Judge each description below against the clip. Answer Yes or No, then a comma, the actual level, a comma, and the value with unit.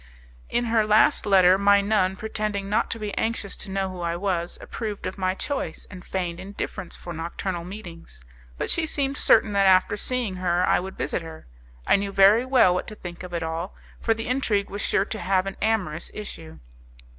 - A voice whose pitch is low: No, high, 195 Hz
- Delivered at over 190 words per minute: Yes, average, 200 wpm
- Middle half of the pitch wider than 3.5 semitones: No, average, 3.0 semitones